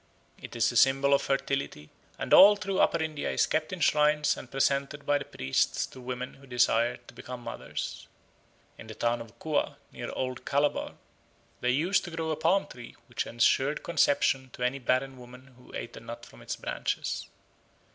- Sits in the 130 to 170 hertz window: Yes, low, 135 Hz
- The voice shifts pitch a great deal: No, average, 3.4 semitones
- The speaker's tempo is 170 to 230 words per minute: Yes, average, 185 wpm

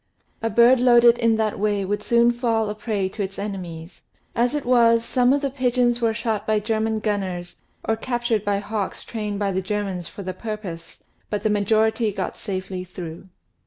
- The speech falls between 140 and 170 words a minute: No, average, 195 wpm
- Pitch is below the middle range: No, high, 215 Hz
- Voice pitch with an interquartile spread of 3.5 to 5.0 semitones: No, average, 3.1 semitones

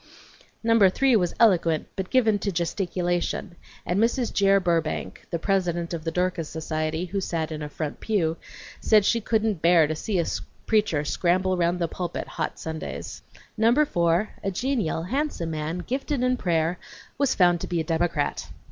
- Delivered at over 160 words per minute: Yes, average, 170 wpm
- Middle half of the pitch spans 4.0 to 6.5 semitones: Yes, average, 4.3 semitones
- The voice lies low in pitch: No, medium, 180 Hz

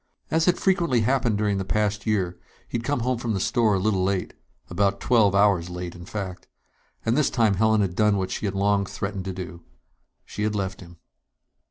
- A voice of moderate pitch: No, low, 100 Hz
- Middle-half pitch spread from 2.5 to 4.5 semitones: Yes, average, 3.0 semitones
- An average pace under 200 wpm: No, fast, 205 wpm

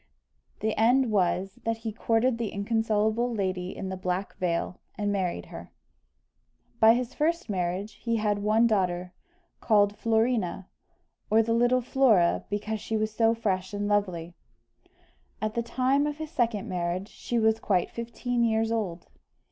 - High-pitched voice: Yes, high, 215 Hz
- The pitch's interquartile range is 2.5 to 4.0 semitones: Yes, average, 3.3 semitones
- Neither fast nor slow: Yes, average, 155 wpm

